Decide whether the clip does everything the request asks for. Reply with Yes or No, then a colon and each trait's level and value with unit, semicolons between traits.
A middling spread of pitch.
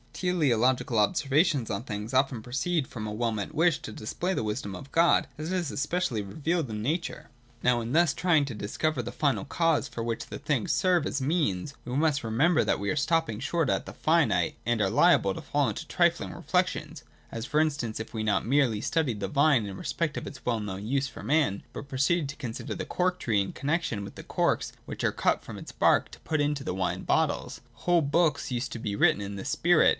No: wide, 6.3 semitones